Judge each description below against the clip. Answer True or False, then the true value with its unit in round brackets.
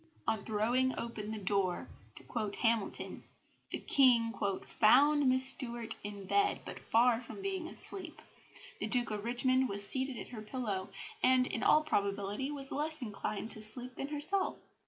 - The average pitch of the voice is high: True (240 Hz)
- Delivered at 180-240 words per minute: False (160 wpm)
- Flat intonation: False (4.0 semitones)